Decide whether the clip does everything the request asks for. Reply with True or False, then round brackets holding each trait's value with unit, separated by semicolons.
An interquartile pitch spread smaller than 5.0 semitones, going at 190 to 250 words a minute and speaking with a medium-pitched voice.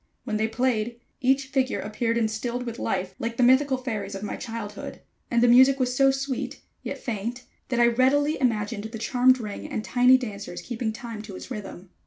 False (3.1 semitones; 195 wpm; 235 Hz)